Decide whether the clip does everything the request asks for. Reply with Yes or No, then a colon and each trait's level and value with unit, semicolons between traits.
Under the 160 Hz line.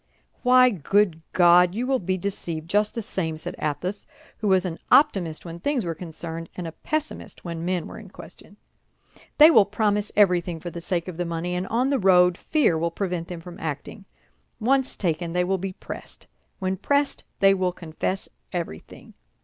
No: medium, 180 Hz